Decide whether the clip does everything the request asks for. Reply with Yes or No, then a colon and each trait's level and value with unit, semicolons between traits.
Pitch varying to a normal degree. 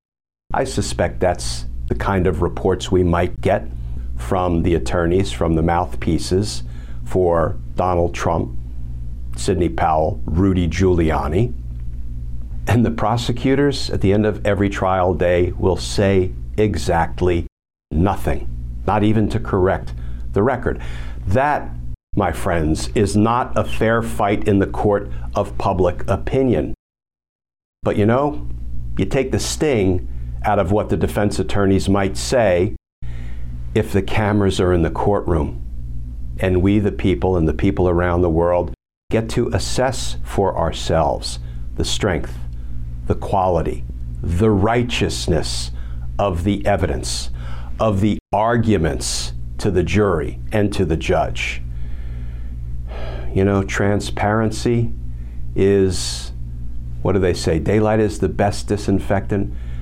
No: wide, 8.9 semitones